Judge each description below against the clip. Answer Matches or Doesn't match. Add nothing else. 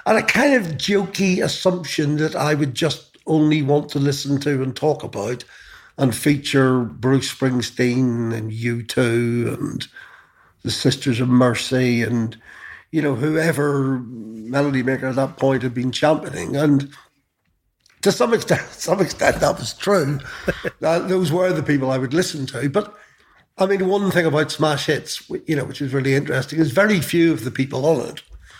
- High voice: Doesn't match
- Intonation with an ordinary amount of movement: Matches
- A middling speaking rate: Matches